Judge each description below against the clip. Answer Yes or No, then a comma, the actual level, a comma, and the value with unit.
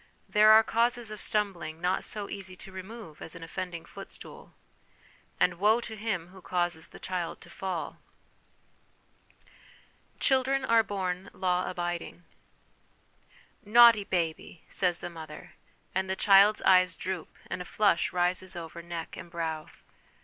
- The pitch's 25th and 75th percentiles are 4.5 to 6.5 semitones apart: No, average, 3.3 semitones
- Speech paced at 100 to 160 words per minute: Yes, average, 140 wpm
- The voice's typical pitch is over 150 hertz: Yes, medium, 185 Hz